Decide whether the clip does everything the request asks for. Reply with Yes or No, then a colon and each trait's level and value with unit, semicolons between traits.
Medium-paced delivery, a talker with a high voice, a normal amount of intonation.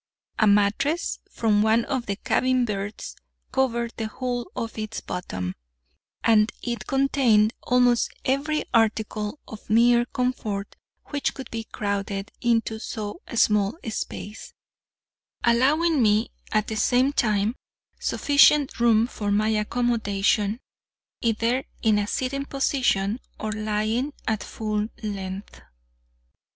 No: slow, 120 wpm; high, 225 Hz; average, 3.0 semitones